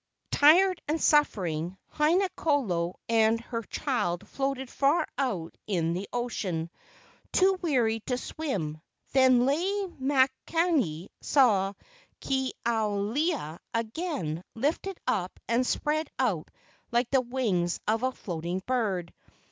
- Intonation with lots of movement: Yes, wide, 7.1 semitones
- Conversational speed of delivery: No, slow, 120 wpm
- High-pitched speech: Yes, high, 240 Hz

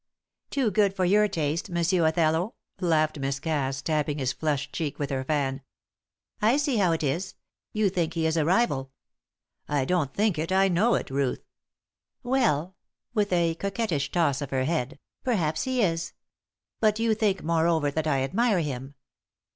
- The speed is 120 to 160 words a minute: No, average, 170 wpm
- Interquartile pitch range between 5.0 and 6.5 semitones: Yes, average, 5.3 semitones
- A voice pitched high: No, medium, 165 Hz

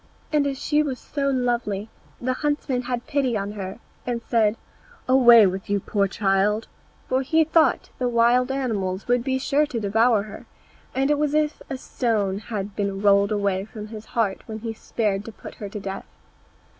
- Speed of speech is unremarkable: Yes, average, 195 wpm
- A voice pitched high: Yes, high, 230 Hz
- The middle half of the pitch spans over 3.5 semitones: Yes, average, 4.4 semitones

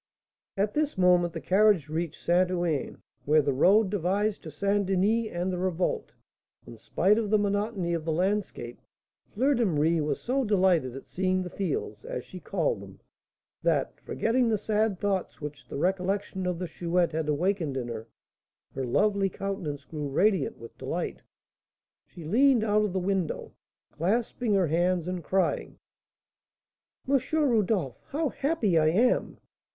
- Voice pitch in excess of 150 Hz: Yes, medium, 185 Hz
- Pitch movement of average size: Yes, average, 4.3 semitones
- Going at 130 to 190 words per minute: Yes, average, 160 wpm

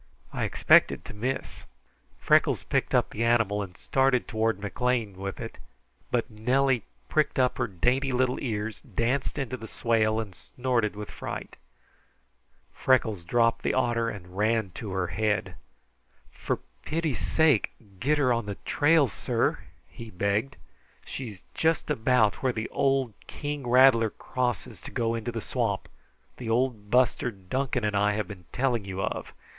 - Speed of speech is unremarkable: Yes, average, 155 wpm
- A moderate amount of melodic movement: Yes, average, 3.6 semitones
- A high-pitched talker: No, low, 115 Hz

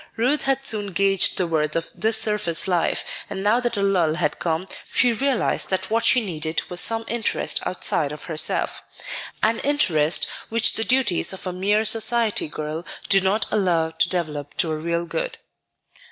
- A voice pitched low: No, high, 190 Hz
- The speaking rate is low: No, average, 180 wpm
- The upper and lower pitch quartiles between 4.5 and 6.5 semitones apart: Yes, average, 5.2 semitones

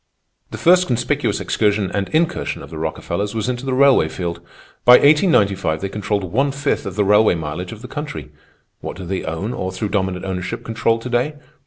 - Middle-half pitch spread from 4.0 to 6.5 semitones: Yes, average, 5.3 semitones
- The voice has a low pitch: Yes, low, 105 Hz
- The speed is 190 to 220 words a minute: Yes, average, 195 wpm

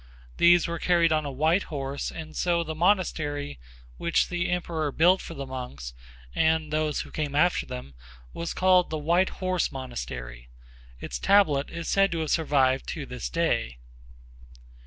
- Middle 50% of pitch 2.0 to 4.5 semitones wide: Yes, average, 4.0 semitones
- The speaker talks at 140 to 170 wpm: Yes, average, 160 wpm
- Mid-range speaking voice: Yes, medium, 155 Hz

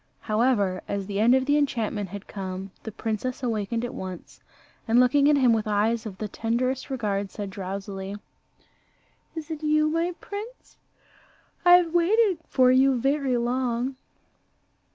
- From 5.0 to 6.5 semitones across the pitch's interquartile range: Yes, wide, 5.6 semitones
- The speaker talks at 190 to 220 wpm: No, average, 155 wpm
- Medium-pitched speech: No, high, 240 Hz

